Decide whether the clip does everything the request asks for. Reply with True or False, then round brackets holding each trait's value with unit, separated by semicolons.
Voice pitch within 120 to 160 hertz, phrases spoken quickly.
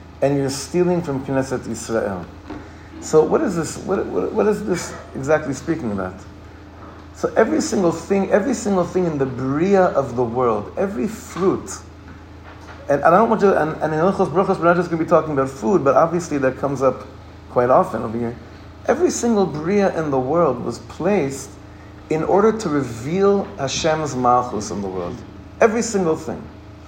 False (140 Hz; 185 wpm)